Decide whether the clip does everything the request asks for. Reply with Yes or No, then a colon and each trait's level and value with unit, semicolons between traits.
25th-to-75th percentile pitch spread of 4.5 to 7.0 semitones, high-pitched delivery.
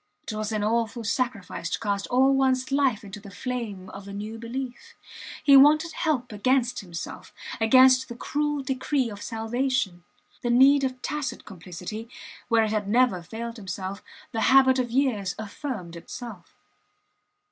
No: average, 4.1 semitones; high, 235 Hz